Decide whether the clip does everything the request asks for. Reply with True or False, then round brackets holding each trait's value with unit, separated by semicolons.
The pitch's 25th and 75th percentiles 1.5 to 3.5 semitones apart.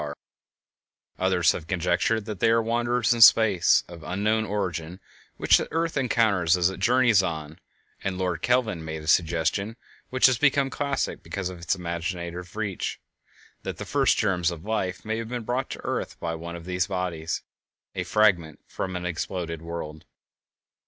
False (4.8 semitones)